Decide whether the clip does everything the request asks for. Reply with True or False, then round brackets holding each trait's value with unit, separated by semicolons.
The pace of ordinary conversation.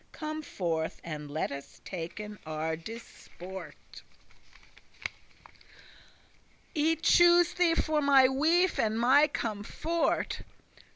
False (95 wpm)